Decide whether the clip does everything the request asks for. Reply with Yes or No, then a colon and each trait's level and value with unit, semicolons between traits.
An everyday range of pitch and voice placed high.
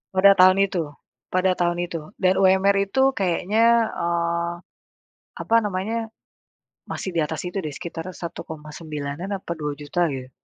No: average, 3.0 semitones; medium, 175 Hz